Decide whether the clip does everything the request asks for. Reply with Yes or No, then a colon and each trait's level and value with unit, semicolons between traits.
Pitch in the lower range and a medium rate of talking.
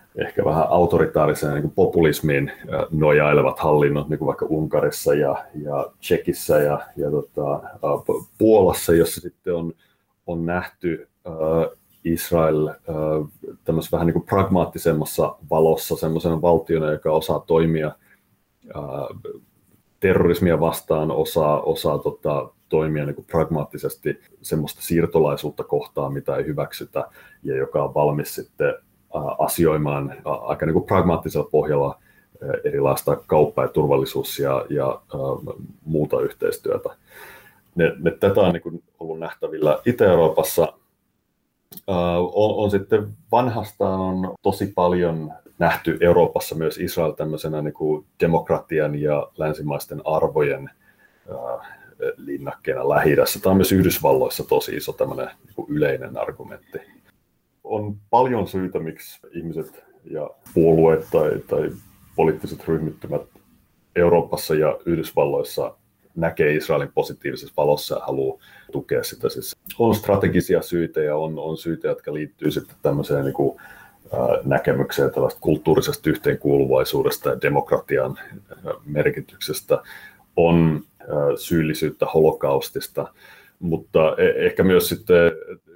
Yes: very low, 95 Hz; average, 115 wpm